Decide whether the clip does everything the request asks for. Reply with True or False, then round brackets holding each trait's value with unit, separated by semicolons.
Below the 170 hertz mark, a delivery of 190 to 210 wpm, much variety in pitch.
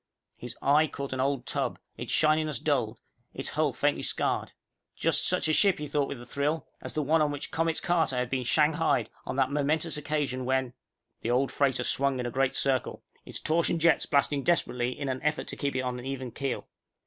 False (140 Hz; 205 wpm; 2.9 semitones)